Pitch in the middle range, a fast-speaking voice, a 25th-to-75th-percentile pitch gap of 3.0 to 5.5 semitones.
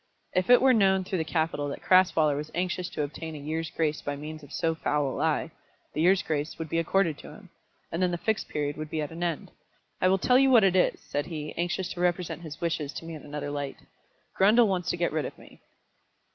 Yes: medium, 165 Hz; fast, 245 wpm; average, 3.4 semitones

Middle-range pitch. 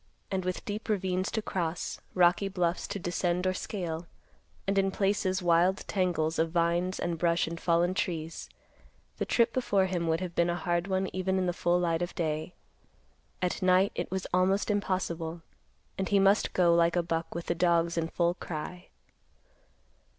Yes: medium, 180 Hz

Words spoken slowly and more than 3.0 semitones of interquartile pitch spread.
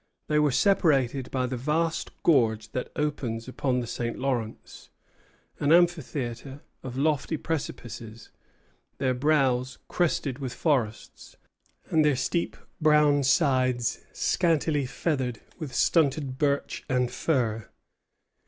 Yes: slow, 115 wpm; average, 3.4 semitones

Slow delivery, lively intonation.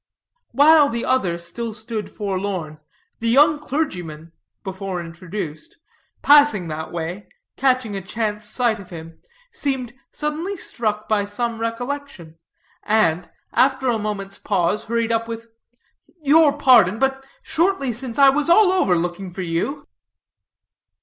Yes: slow, 130 wpm; wide, 6.5 semitones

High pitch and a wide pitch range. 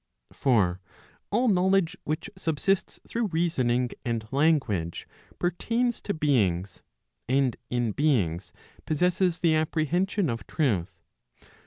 No: medium, 150 Hz; wide, 7.4 semitones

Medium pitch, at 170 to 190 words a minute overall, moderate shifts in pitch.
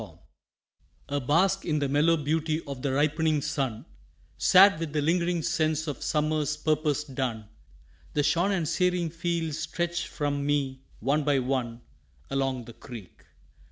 No: medium, 150 Hz; average, 150 wpm; average, 3.1 semitones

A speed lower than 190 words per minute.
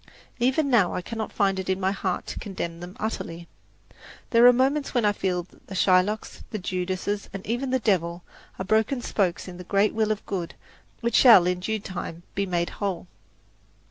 No: average, 195 wpm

